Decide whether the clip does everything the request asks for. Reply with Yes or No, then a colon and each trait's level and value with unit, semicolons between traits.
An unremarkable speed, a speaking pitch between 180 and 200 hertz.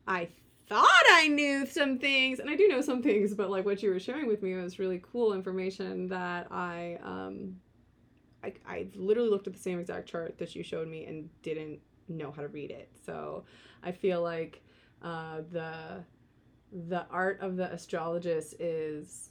Yes: average, 185 wpm; medium, 185 Hz